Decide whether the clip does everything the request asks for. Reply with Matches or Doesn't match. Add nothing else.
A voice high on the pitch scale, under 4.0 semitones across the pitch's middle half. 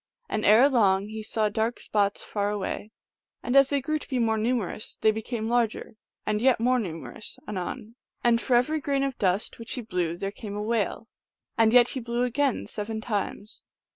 Matches